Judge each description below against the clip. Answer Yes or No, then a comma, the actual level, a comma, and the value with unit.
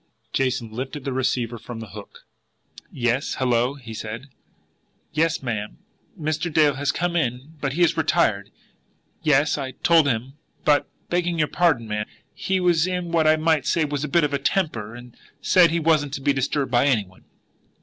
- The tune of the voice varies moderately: Yes, average, 4.6 semitones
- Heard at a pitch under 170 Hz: Yes, medium, 140 Hz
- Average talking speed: Yes, average, 180 wpm